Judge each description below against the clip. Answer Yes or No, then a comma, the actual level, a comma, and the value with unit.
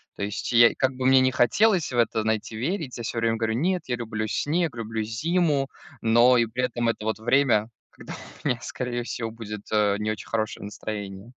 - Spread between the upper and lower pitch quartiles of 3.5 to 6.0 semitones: No, average, 2.9 semitones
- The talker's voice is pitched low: Yes, low, 115 Hz